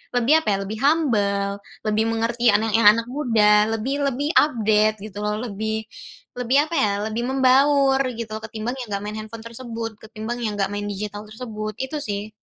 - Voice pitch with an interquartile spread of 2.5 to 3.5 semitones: Yes, average, 2.8 semitones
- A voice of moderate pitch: No, high, 220 Hz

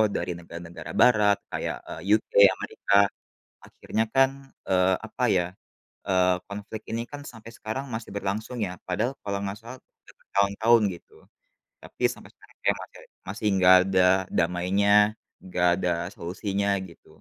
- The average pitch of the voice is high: No, low, 100 Hz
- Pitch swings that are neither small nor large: Yes, average, 3.2 semitones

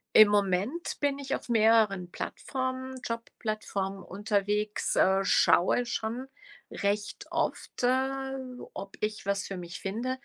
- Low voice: No, high, 215 Hz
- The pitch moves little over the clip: No, average, 4.5 semitones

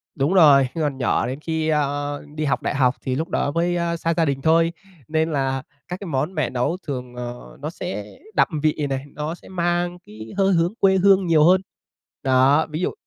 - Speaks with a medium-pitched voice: Yes, medium, 155 Hz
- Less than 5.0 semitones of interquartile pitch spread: Yes, average, 4.1 semitones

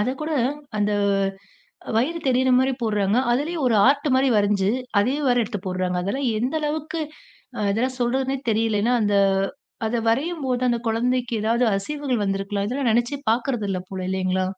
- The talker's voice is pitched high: Yes, high, 240 Hz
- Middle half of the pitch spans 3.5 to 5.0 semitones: Yes, average, 4.4 semitones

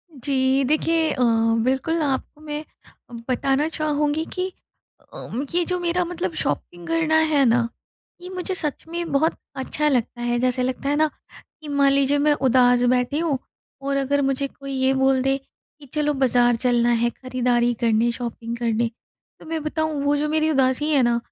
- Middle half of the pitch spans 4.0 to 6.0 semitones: No, average, 3.6 semitones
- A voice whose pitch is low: No, very high, 275 Hz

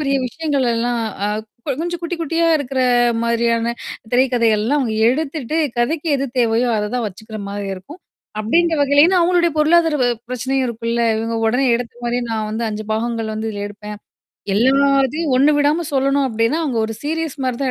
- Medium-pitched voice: No, very high, 255 Hz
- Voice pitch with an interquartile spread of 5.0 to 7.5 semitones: No, average, 4.5 semitones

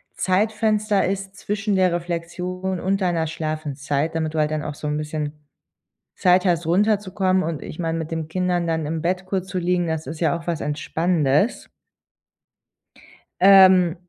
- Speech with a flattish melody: No, average, 3.0 semitones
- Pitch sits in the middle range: Yes, medium, 175 Hz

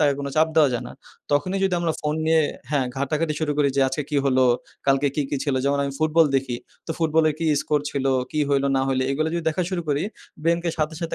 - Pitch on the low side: No, medium, 150 Hz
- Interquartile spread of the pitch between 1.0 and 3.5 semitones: Yes, narrow, 2.5 semitones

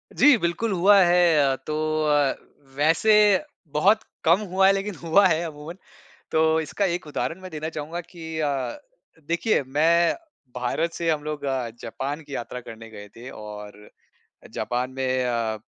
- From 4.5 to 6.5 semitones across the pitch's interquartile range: Yes, average, 4.8 semitones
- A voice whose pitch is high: No, medium, 155 Hz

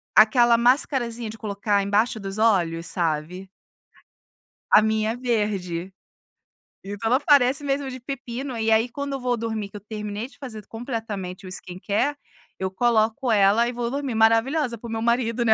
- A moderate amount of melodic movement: Yes, average, 3.2 semitones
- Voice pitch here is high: Yes, high, 225 Hz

